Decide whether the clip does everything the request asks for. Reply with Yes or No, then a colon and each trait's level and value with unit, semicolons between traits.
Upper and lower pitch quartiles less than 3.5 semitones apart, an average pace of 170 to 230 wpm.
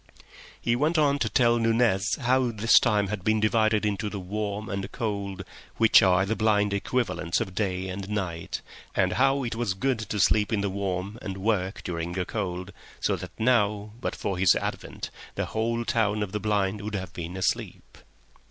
Yes: average, 2.9 semitones; average, 190 wpm